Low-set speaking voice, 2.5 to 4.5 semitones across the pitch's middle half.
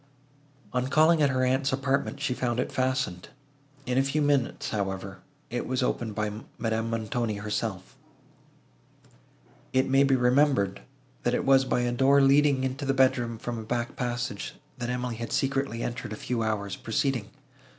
Yes: low, 125 Hz; average, 3.0 semitones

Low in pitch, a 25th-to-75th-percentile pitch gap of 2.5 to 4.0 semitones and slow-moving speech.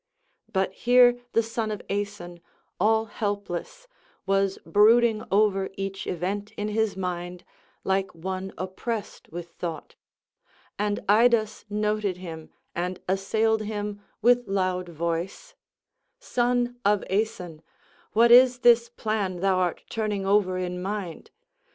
No: high, 205 Hz; average, 3.1 semitones; slow, 120 wpm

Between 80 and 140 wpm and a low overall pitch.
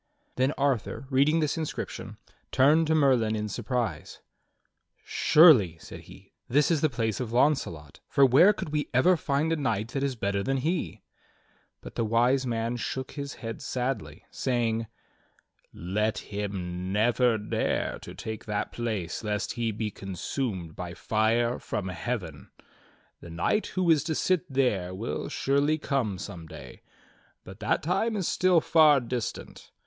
No: average, 155 wpm; low, 120 Hz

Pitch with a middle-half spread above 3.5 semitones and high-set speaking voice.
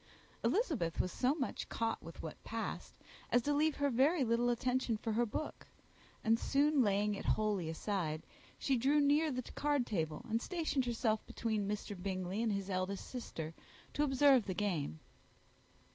Yes: wide, 5.4 semitones; high, 230 Hz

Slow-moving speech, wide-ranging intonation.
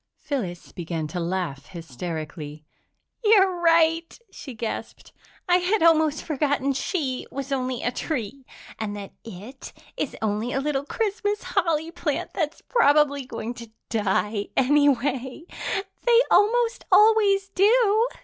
Yes: slow, 125 wpm; wide, 8.4 semitones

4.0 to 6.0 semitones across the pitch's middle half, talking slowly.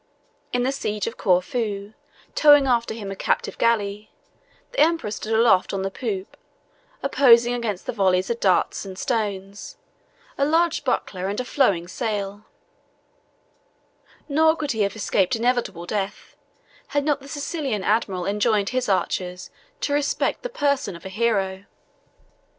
No: average, 5.2 semitones; average, 145 wpm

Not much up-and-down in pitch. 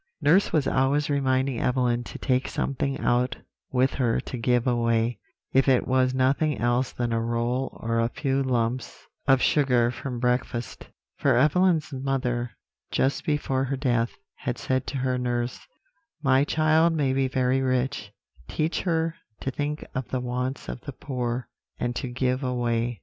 Yes: narrow, 2.0 semitones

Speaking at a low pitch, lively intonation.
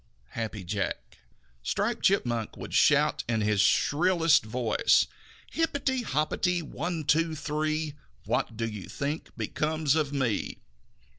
No: medium, 150 Hz; wide, 6.1 semitones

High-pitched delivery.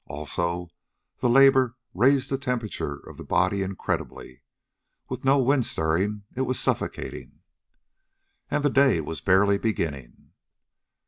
No: low, 105 Hz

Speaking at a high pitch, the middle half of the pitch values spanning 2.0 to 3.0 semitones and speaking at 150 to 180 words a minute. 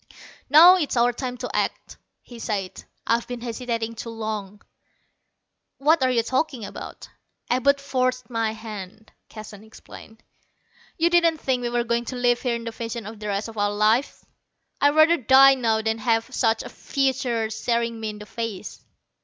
Yes: high, 235 Hz; average, 2.7 semitones; average, 170 wpm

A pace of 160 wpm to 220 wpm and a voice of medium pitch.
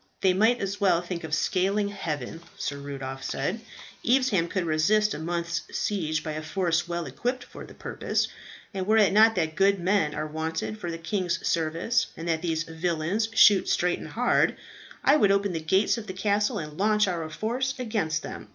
Yes: average, 195 wpm; medium, 180 Hz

